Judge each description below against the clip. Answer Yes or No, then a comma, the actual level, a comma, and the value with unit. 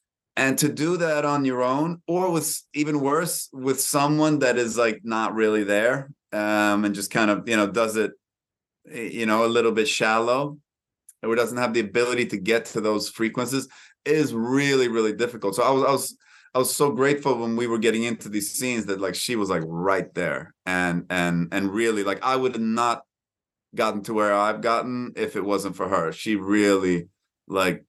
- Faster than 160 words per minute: Yes, average, 200 wpm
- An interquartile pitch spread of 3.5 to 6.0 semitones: Yes, average, 4.1 semitones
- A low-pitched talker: Yes, low, 115 Hz